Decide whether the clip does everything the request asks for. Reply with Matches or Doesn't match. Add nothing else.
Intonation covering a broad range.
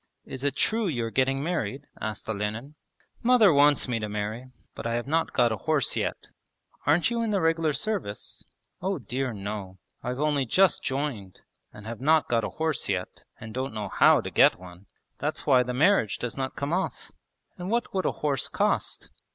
Matches